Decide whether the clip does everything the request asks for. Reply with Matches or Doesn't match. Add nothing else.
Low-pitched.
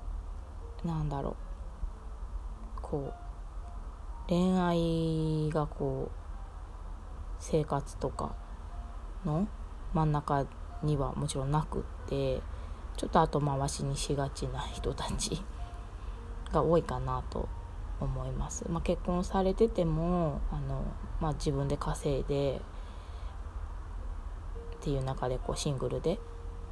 Matches